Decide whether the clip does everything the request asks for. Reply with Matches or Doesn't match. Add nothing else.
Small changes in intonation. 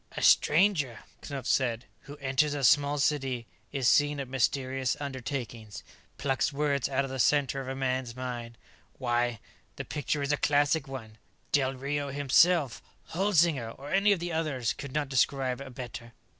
Matches